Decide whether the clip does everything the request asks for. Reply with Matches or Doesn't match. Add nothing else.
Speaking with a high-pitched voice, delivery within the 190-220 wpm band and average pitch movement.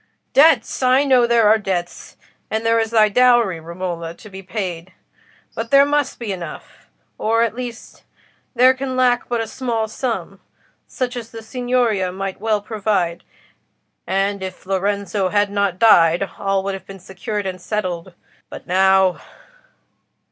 Doesn't match